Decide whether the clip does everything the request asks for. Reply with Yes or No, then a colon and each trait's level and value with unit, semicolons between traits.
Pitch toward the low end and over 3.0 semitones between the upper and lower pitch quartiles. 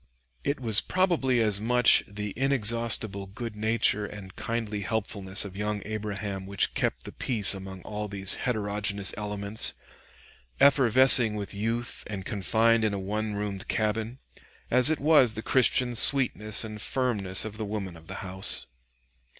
No: low, 105 Hz; narrow, 2.6 semitones